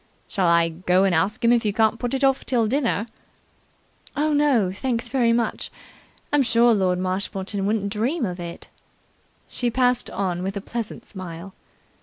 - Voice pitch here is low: No, high, 215 Hz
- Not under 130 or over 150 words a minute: No, average, 175 wpm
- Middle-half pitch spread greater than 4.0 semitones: Yes, average, 4.5 semitones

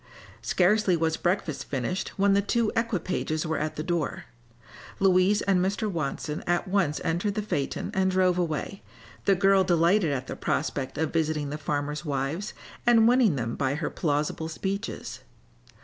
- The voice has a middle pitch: Yes, medium, 175 Hz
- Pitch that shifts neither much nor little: Yes, average, 4.5 semitones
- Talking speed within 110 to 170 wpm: Yes, average, 160 wpm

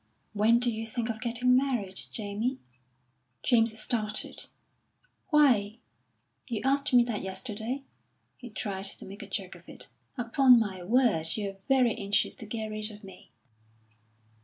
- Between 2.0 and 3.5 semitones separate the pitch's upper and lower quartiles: Yes, average, 3.2 semitones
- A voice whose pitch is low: No, high, 225 Hz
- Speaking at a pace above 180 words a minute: No, average, 145 wpm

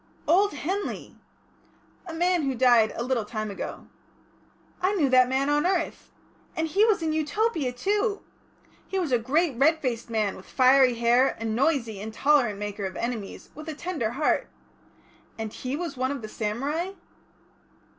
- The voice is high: Yes, very high, 270 Hz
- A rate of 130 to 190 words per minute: Yes, average, 165 wpm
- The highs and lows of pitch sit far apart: Yes, wide, 5.8 semitones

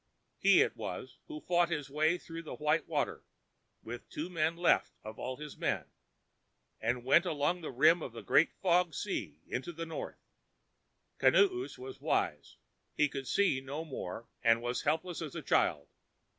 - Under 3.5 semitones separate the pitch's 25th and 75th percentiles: No, average, 4.8 semitones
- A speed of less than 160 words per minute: No, average, 170 wpm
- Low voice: No, medium, 155 Hz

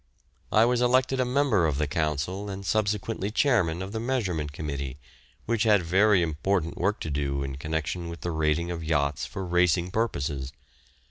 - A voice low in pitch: Yes, very low, 90 Hz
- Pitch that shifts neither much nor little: No, wide, 5.7 semitones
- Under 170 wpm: No, average, 175 wpm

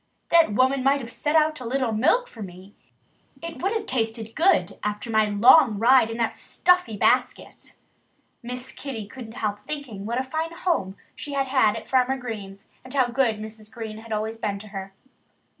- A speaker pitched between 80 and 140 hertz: No, high, 235 Hz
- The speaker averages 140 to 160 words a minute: No, average, 190 wpm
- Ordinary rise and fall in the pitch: Yes, average, 4.3 semitones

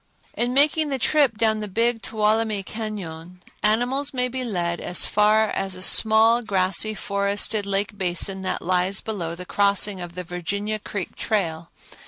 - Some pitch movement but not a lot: Yes, average, 3.3 semitones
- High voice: Yes, high, 210 Hz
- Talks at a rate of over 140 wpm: Yes, average, 160 wpm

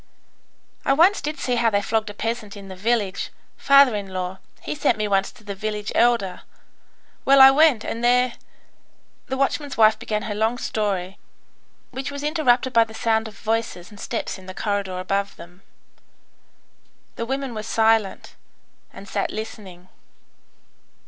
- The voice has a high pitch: Yes, high, 220 Hz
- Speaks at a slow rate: No, average, 165 wpm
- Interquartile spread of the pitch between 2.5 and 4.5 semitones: Yes, average, 3.5 semitones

